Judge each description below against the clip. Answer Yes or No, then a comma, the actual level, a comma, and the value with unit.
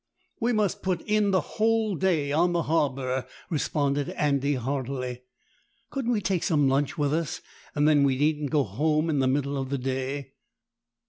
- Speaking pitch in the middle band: Yes, medium, 145 Hz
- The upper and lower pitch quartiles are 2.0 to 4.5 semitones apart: Yes, average, 4.1 semitones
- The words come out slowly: No, average, 175 wpm